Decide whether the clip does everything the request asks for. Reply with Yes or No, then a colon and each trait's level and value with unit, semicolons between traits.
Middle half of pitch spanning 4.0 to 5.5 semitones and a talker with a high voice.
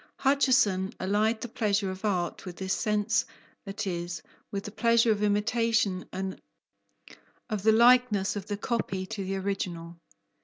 No: average, 2.7 semitones; high, 205 Hz